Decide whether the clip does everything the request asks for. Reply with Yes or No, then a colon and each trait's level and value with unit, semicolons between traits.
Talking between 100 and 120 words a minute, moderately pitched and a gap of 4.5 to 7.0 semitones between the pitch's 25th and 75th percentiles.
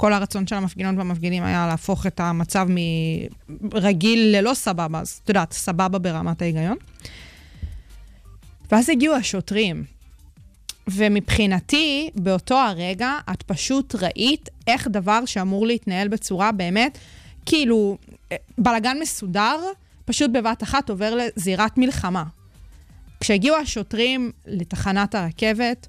No: average, 105 wpm; high, 200 Hz; average, 5.0 semitones